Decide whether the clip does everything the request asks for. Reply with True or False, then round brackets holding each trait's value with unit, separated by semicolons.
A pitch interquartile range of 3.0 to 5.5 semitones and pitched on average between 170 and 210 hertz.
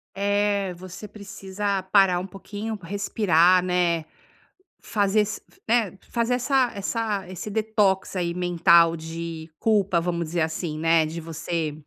True (3.4 semitones; 190 Hz)